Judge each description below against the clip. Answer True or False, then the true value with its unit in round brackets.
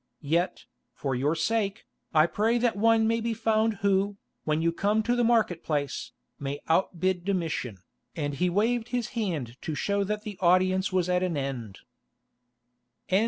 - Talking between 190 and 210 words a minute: False (165 wpm)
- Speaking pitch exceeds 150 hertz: True (190 Hz)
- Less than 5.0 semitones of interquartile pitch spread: False (5.3 semitones)